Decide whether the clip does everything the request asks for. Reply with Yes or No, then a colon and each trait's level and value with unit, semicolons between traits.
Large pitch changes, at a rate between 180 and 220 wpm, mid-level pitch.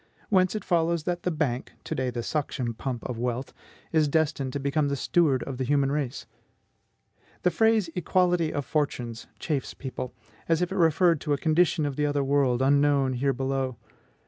No: average, 3.7 semitones; average, 185 wpm; medium, 145 Hz